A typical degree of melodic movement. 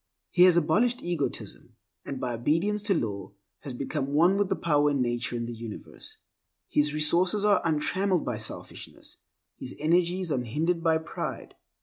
No: wide, 5.9 semitones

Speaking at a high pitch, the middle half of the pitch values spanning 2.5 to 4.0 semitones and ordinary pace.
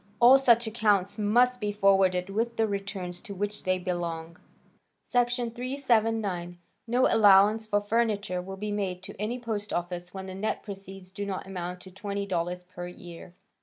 Yes: high, 200 Hz; average, 3.4 semitones; average, 165 wpm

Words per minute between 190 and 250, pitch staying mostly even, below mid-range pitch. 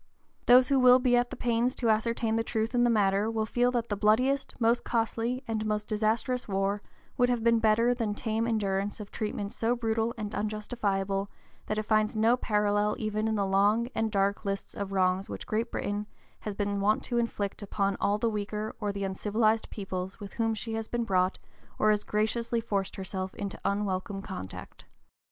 No: average, 195 wpm; narrow, 2.3 semitones; high, 215 Hz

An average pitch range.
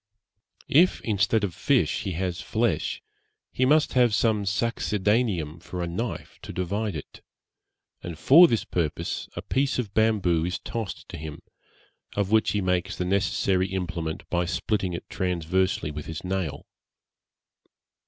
Yes: average, 4.0 semitones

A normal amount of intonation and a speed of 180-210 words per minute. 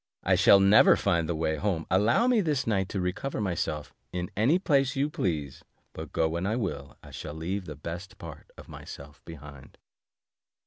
No: wide, 5.9 semitones; average, 185 wpm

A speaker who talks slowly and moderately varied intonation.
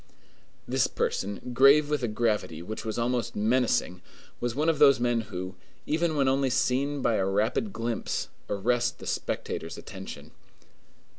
No: average, 150 wpm; average, 4.2 semitones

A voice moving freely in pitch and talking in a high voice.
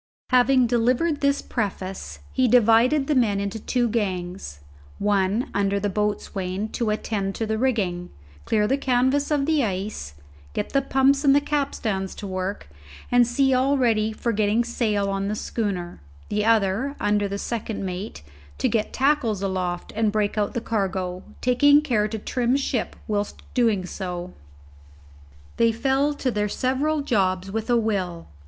No: average, 4.4 semitones; high, 220 Hz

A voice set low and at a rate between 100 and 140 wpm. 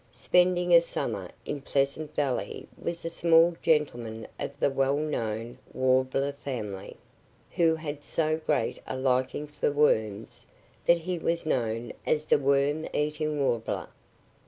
No: medium, 145 Hz; slow, 135 wpm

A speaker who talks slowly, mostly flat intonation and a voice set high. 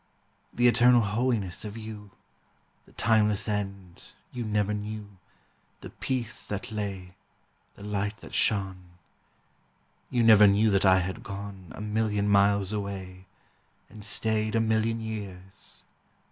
No: slow, 130 wpm; narrow, 1.9 semitones; low, 105 Hz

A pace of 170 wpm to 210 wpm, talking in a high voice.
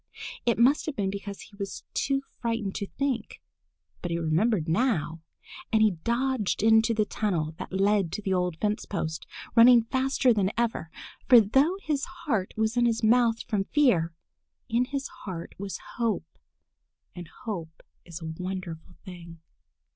No: average, 160 wpm; high, 210 Hz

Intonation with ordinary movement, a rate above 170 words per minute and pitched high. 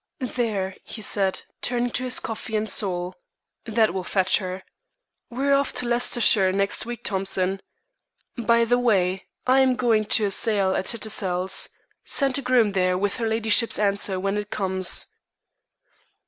No: average, 3.9 semitones; average, 160 wpm; high, 215 Hz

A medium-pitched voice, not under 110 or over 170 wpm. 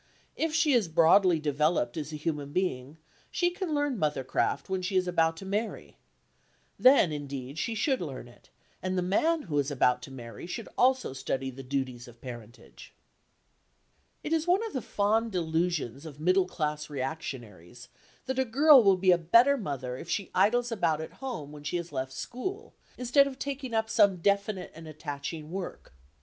No: medium, 170 Hz; average, 180 wpm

